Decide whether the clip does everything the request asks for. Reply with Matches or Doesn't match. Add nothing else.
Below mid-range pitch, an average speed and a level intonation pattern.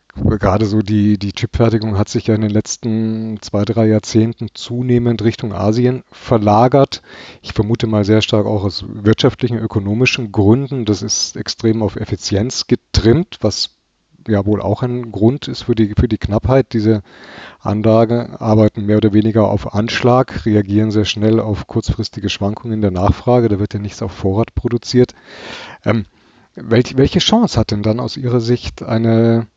Matches